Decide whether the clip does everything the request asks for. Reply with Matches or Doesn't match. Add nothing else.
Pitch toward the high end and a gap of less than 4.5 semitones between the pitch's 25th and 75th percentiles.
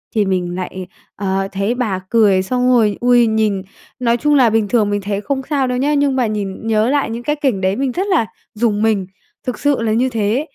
Matches